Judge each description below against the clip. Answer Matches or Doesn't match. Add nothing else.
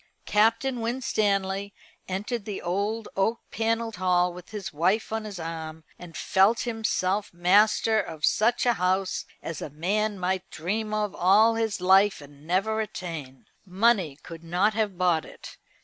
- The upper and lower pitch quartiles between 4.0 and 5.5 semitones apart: Doesn't match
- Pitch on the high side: Matches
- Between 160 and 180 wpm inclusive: Doesn't match